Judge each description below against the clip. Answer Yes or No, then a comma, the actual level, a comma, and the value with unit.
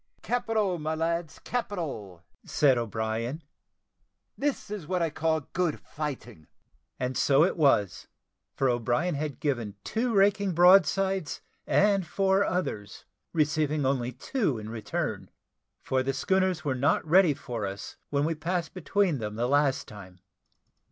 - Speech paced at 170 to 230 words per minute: No, average, 140 wpm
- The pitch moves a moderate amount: No, wide, 6.6 semitones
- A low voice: No, medium, 150 Hz